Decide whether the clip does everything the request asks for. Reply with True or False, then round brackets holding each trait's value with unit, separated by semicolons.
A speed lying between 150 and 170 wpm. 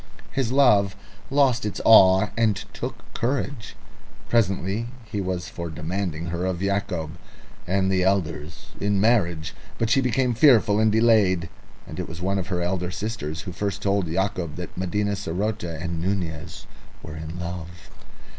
True (155 wpm)